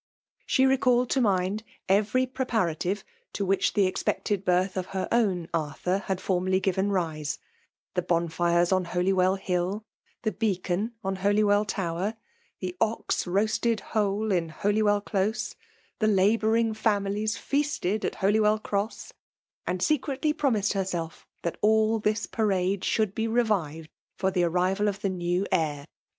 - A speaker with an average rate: Yes, average, 145 wpm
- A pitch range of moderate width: Yes, average, 3.1 semitones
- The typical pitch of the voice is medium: No, high, 200 Hz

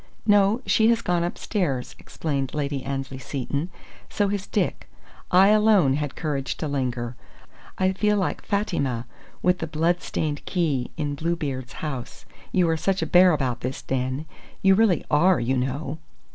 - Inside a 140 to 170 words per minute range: Yes, average, 160 wpm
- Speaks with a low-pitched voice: No, medium, 155 Hz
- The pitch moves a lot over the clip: Yes, wide, 5.7 semitones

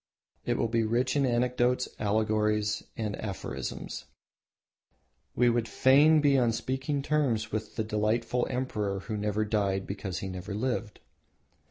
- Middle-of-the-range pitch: No, low, 110 Hz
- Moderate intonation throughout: Yes, average, 3.1 semitones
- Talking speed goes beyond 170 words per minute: No, average, 145 wpm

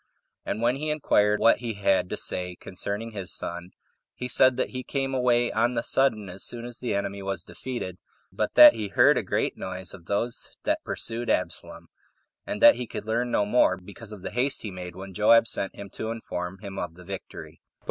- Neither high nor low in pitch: No, low, 105 Hz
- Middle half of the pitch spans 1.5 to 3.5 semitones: No, average, 4.1 semitones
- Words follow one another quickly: Yes, fast, 210 wpm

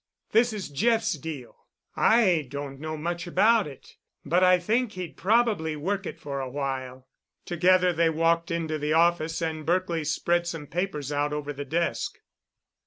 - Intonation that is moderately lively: Yes, average, 3.7 semitones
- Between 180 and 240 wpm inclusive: No, average, 165 wpm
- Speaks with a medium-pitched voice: Yes, medium, 165 Hz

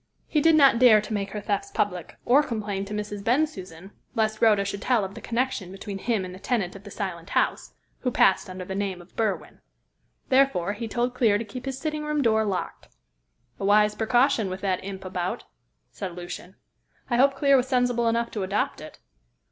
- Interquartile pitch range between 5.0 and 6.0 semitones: No, average, 4.3 semitones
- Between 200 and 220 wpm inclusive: Yes, fast, 205 wpm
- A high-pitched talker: Yes, high, 210 Hz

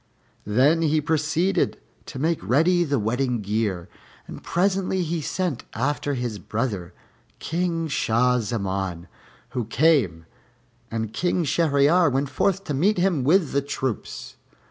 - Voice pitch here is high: No, medium, 140 Hz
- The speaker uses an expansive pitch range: Yes, wide, 6.6 semitones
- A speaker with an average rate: No, slow, 130 wpm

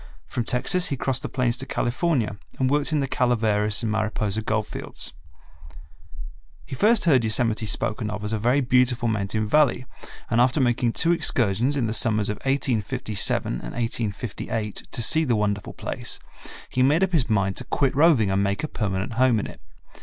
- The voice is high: No, low, 120 Hz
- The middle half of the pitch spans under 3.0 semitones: No, average, 3.9 semitones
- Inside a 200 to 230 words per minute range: No, average, 185 wpm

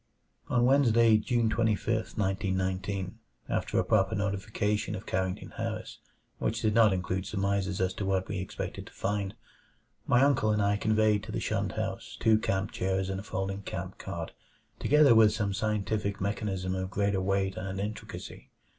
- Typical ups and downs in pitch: No, narrow, 2.2 semitones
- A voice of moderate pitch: No, low, 100 Hz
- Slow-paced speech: No, average, 165 wpm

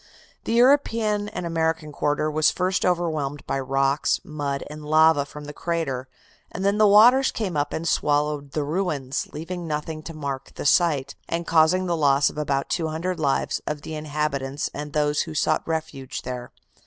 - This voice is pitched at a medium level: Yes, medium, 155 Hz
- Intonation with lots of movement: No, average, 2.8 semitones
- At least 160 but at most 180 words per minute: Yes, average, 175 wpm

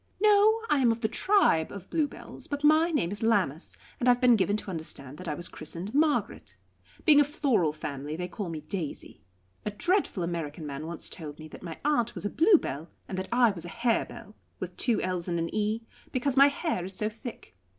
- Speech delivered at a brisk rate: Yes, fast, 215 wpm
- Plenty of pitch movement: Yes, wide, 8.4 semitones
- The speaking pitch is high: Yes, high, 210 Hz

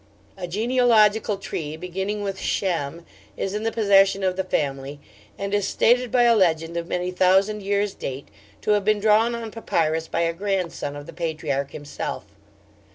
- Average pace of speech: Yes, average, 170 wpm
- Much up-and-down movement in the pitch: No, average, 4.1 semitones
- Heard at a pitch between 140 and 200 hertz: Yes, high, 190 Hz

